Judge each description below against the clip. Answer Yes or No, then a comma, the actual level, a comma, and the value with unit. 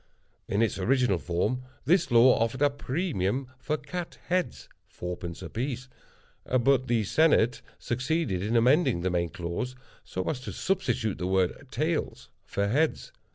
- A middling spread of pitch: No, wide, 6.7 semitones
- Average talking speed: Yes, average, 150 wpm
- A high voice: No, low, 125 Hz